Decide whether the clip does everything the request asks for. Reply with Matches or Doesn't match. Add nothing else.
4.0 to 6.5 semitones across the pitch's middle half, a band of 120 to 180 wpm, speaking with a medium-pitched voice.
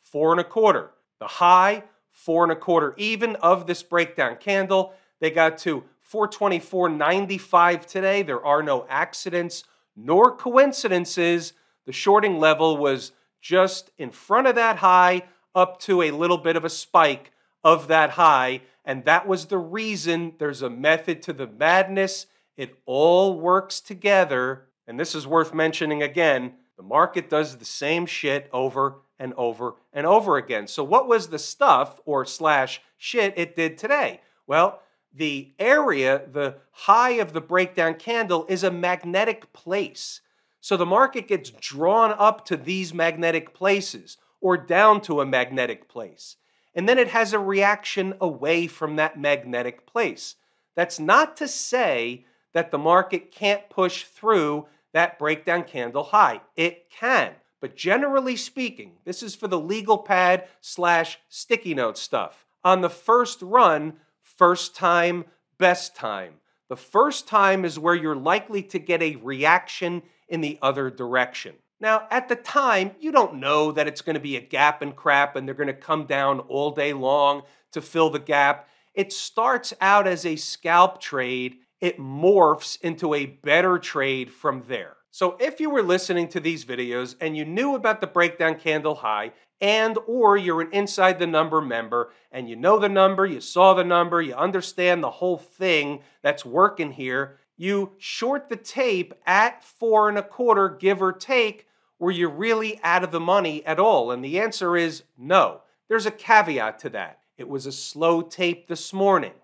Matches